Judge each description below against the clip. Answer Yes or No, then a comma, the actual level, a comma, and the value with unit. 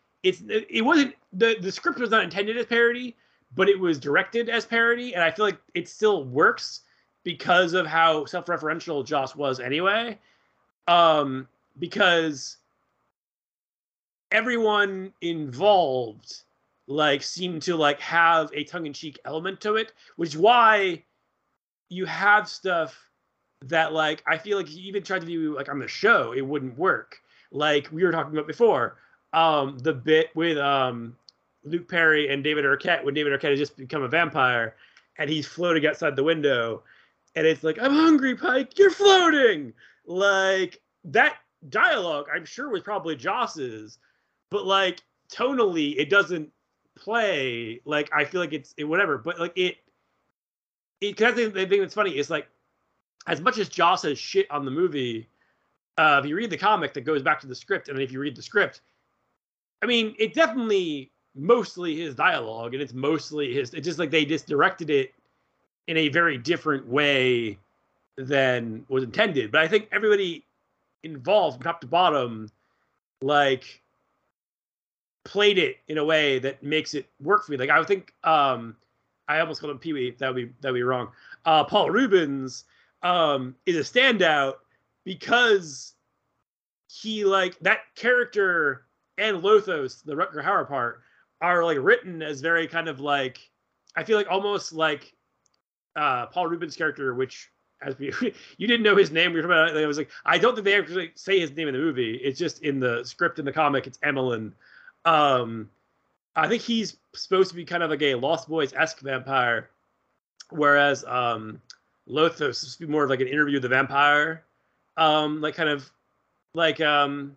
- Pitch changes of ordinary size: No, wide, 5.8 semitones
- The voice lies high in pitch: No, medium, 160 Hz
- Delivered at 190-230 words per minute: No, average, 170 wpm